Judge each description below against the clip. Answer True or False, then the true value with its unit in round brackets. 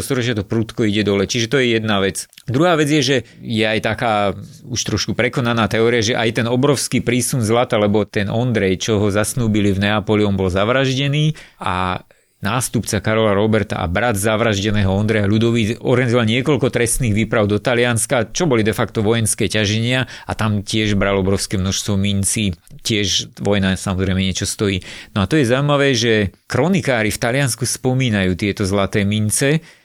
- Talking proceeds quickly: True (170 wpm)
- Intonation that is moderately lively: True (3.3 semitones)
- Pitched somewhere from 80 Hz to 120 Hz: True (110 Hz)